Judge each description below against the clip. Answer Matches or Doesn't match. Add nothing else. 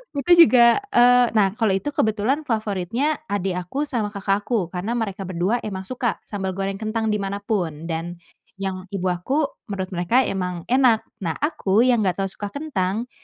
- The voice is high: Matches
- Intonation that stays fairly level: Doesn't match